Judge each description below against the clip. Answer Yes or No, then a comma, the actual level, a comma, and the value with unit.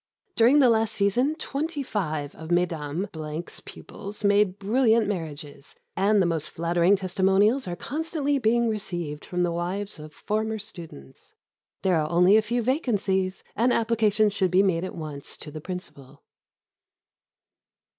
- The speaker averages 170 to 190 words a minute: No, average, 145 wpm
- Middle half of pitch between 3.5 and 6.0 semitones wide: Yes, average, 4.6 semitones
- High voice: Yes, high, 195 Hz